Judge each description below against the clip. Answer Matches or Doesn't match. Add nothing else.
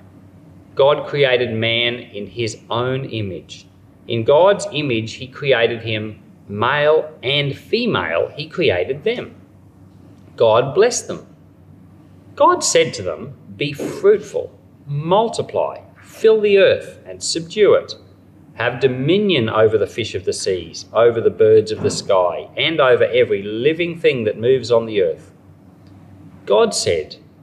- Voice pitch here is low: Doesn't match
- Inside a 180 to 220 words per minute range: Doesn't match